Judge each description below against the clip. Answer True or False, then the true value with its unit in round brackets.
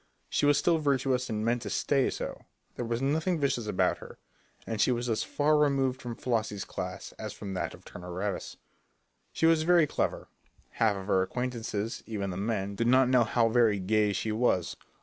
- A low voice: True (120 Hz)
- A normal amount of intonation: True (4.2 semitones)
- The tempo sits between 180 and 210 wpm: True (195 wpm)